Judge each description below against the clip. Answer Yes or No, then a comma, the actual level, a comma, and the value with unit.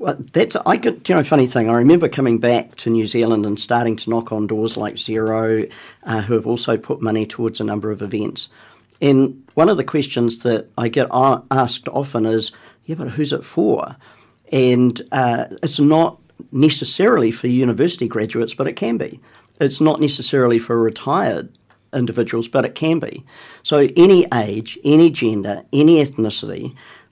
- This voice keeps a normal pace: Yes, average, 175 wpm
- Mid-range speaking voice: No, low, 120 Hz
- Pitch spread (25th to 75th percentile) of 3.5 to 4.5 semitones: Yes, average, 3.8 semitones